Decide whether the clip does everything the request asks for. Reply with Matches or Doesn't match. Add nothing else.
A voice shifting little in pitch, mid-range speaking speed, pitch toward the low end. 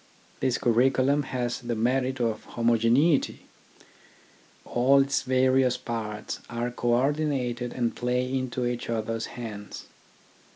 Doesn't match